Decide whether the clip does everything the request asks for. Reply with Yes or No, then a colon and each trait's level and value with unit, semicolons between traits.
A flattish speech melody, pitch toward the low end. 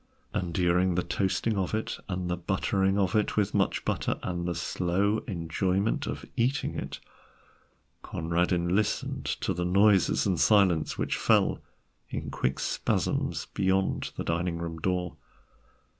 Yes: narrow, 2.2 semitones; very low, 90 Hz